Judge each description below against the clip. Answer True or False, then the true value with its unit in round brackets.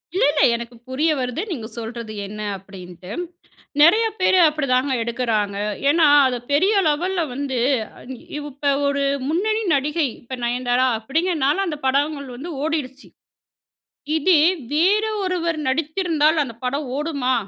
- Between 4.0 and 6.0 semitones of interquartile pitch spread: True (4.5 semitones)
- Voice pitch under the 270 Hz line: False (285 Hz)